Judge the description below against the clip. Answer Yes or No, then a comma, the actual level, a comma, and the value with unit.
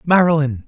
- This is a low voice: No, medium, 150 Hz